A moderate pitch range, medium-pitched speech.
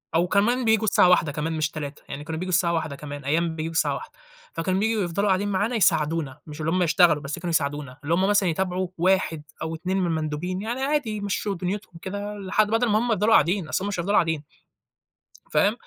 Yes: average, 4.2 semitones; medium, 180 Hz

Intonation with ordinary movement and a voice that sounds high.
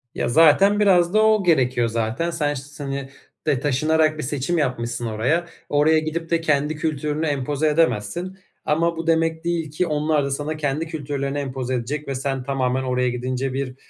No: average, 3.6 semitones; medium, 145 Hz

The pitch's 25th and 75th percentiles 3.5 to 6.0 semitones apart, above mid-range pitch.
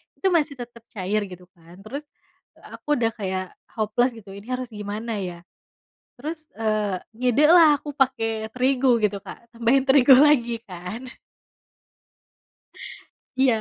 Yes: average, 4.3 semitones; high, 235 Hz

